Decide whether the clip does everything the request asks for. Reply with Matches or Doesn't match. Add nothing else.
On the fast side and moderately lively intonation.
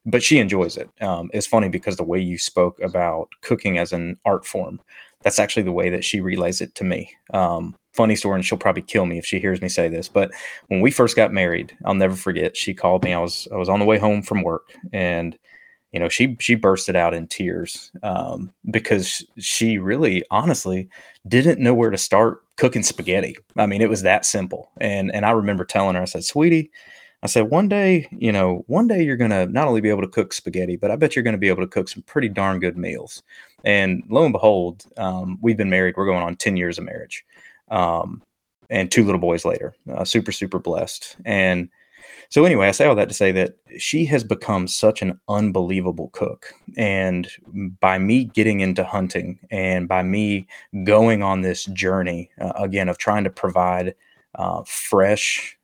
Matches